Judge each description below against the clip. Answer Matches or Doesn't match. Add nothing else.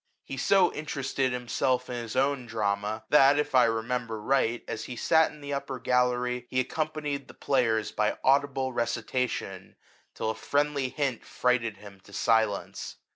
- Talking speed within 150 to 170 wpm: Matches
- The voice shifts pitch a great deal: Doesn't match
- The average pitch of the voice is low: Matches